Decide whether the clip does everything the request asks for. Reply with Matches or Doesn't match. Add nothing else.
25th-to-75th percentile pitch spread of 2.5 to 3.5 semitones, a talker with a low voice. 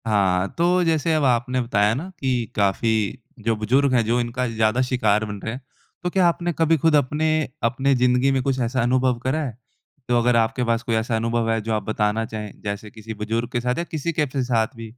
Matches